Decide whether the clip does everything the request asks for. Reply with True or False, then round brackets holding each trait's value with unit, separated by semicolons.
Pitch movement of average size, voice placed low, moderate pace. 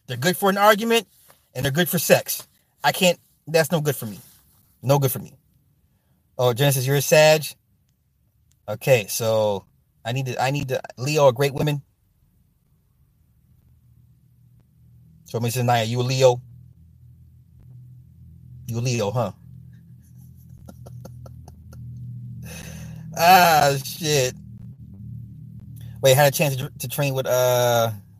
False (3.0 semitones; 125 Hz; 125 wpm)